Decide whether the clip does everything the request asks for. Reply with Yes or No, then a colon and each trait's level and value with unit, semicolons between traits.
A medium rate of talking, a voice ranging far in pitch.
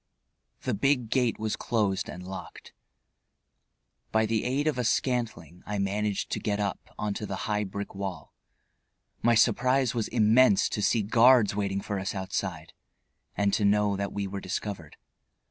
No: average, 160 wpm; average, 2.9 semitones